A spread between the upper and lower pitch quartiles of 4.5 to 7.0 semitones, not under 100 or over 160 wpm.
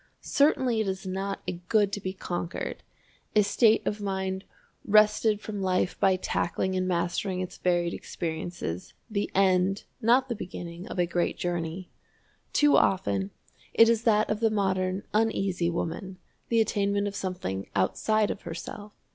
No: average, 3.1 semitones; average, 155 wpm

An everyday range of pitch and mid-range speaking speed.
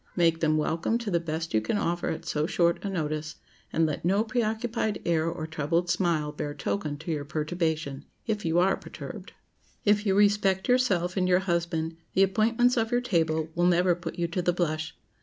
Yes: average, 3.8 semitones; average, 195 wpm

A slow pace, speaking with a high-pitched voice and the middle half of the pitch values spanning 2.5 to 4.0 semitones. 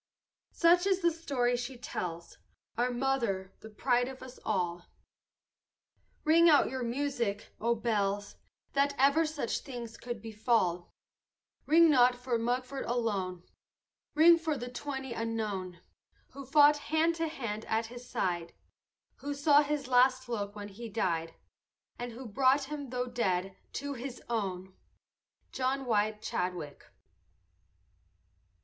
No: slow, 130 wpm; high, 245 Hz; average, 4.9 semitones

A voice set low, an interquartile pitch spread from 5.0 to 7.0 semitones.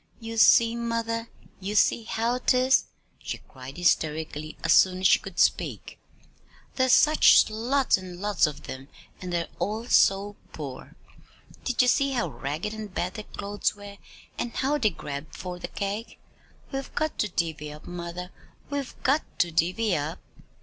No: high, 205 Hz; average, 5.3 semitones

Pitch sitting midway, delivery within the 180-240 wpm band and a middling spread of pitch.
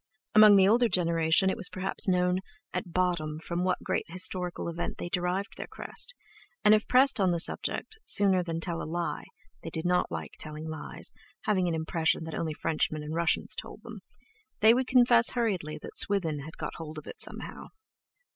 Yes: medium, 180 Hz; average, 185 wpm; average, 3.9 semitones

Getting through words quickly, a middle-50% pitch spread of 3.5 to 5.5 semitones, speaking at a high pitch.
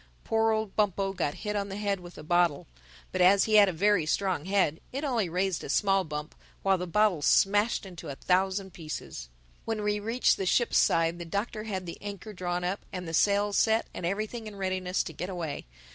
No: fast, 215 wpm; average, 3.0 semitones; high, 195 Hz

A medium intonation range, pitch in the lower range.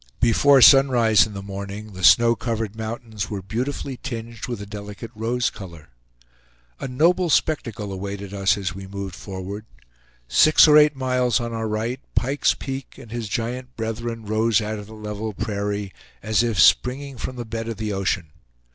Yes: average, 3.3 semitones; low, 110 Hz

